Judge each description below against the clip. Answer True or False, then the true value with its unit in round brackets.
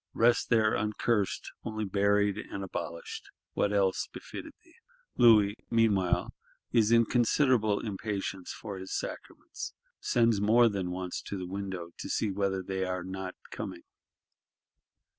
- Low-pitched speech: True (100 Hz)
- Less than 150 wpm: True (135 wpm)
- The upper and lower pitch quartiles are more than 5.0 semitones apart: False (2.6 semitones)